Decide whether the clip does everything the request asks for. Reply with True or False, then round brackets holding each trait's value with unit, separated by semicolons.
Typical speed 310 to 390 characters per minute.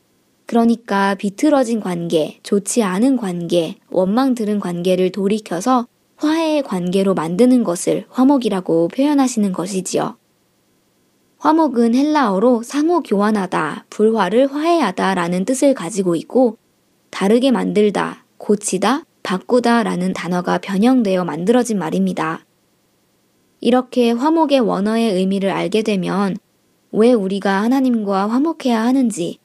False (285 characters per minute)